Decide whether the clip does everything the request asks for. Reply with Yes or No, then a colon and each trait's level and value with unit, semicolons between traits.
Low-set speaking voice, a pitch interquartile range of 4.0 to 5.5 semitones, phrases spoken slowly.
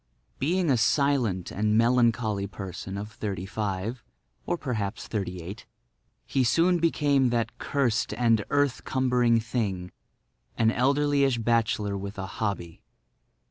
Yes: low, 115 Hz; average, 4.7 semitones; slow, 110 wpm